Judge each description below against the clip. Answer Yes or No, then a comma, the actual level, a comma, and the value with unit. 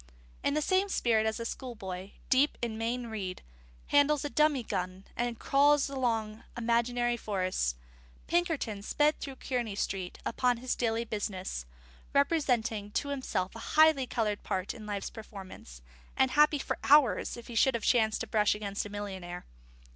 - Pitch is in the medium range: No, high, 230 Hz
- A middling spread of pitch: Yes, average, 4.7 semitones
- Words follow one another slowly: No, average, 160 wpm